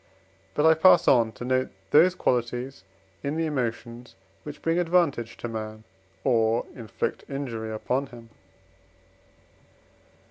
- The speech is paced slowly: Yes, slow, 120 wpm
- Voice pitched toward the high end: No, low, 125 Hz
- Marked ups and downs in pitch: No, average, 4.3 semitones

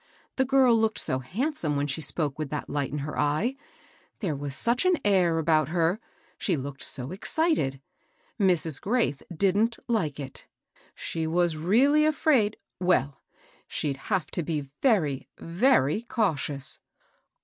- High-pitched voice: No, medium, 170 Hz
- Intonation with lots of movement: Yes, wide, 7.4 semitones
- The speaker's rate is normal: Yes, average, 160 wpm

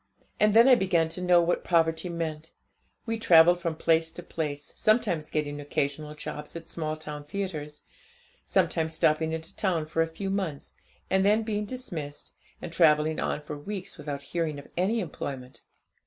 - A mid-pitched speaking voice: Yes, medium, 160 Hz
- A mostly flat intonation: No, average, 3.4 semitones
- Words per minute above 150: Yes, average, 170 wpm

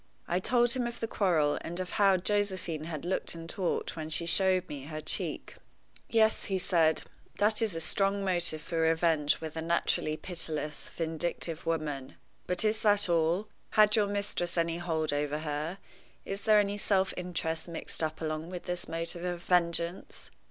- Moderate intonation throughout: Yes, average, 3.5 semitones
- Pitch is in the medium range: Yes, medium, 170 Hz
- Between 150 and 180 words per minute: Yes, average, 175 wpm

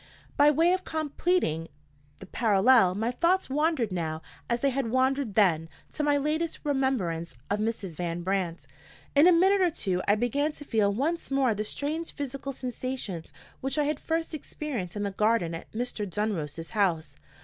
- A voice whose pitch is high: Yes, high, 245 Hz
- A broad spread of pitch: Yes, wide, 7.4 semitones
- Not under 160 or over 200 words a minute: Yes, average, 170 wpm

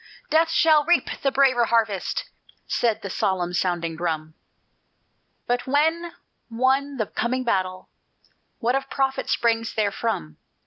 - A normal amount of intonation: No, wide, 6.4 semitones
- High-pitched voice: Yes, high, 235 Hz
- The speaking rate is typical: No, slow, 125 wpm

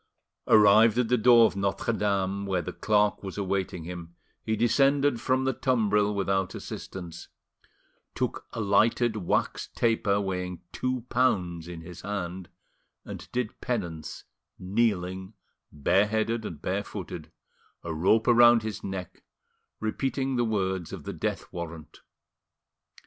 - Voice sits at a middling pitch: No, low, 100 Hz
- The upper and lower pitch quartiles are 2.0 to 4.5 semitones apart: Yes, average, 4.0 semitones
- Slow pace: Yes, slow, 130 wpm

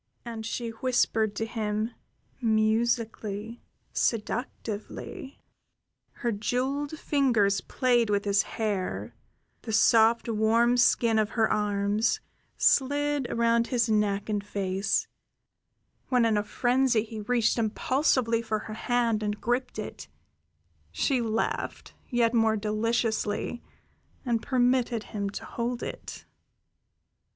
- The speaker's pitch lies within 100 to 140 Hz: No, high, 225 Hz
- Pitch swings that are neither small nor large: No, narrow, 2.3 semitones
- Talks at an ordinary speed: No, slow, 110 wpm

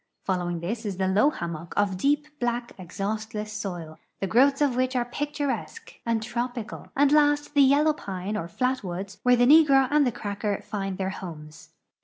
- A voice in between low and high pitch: No, high, 220 Hz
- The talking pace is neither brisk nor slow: Yes, average, 185 wpm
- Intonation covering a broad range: Yes, wide, 6.1 semitones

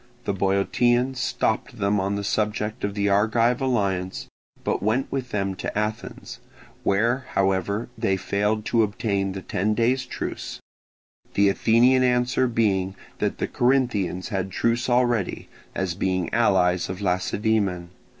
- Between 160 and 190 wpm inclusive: No, average, 140 wpm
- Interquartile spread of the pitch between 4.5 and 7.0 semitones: No, average, 3.6 semitones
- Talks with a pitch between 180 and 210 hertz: No, low, 105 Hz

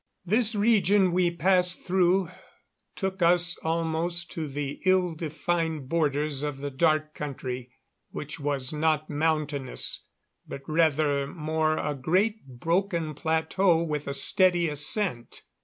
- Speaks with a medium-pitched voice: Yes, medium, 160 Hz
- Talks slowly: Yes, slow, 125 wpm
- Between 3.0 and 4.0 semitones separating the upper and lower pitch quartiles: Yes, average, 3.3 semitones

